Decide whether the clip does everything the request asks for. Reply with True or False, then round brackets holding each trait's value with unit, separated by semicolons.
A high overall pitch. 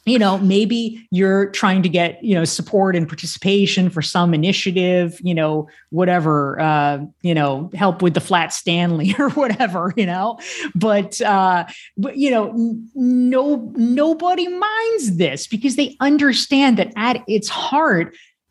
True (195 Hz)